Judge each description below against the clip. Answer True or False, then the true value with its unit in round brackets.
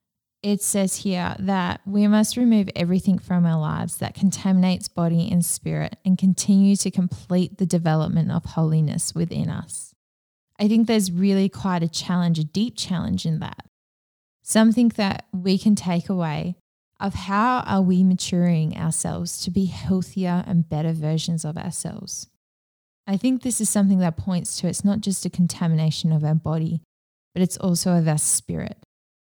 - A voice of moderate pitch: True (180 Hz)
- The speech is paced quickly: False (165 wpm)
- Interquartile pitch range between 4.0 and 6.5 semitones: False (3.2 semitones)